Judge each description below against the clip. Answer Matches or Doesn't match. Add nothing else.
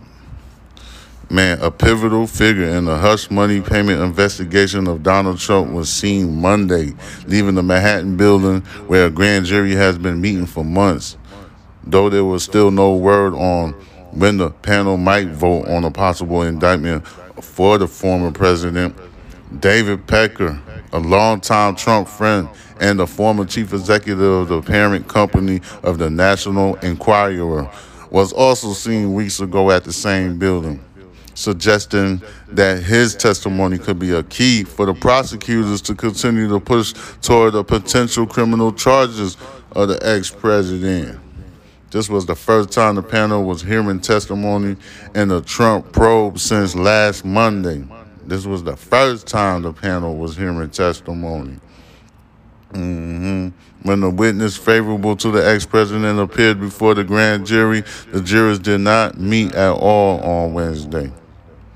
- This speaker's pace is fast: Doesn't match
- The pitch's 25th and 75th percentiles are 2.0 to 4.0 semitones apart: Matches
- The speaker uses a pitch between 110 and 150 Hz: Doesn't match